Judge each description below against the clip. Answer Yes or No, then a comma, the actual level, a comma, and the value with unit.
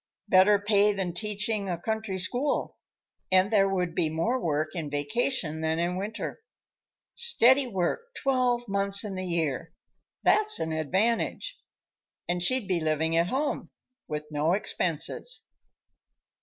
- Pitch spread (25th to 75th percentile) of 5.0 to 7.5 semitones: Yes, wide, 5.5 semitones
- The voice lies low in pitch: No, high, 195 Hz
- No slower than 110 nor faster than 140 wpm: Yes, slow, 135 wpm